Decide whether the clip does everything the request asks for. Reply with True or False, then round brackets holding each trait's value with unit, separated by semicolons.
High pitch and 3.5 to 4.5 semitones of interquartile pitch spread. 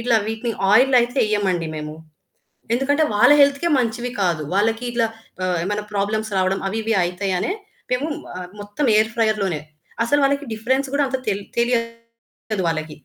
True (225 Hz; 4.0 semitones)